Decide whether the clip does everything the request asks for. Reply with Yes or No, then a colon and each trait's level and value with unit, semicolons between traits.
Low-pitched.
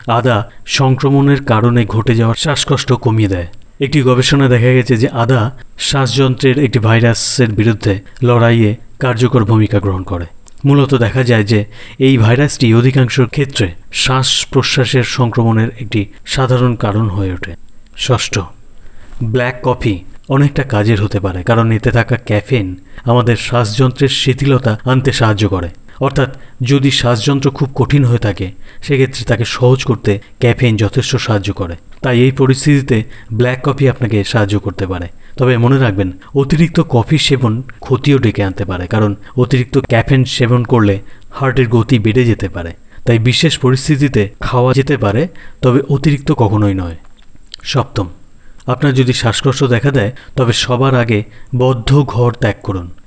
Yes: low, 120 Hz